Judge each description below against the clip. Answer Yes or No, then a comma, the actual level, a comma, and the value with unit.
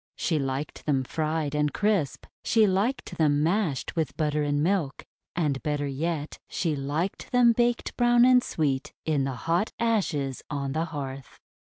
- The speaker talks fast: No, average, 160 wpm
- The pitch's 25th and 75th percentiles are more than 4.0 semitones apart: Yes, average, 5.3 semitones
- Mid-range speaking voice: Yes, medium, 155 Hz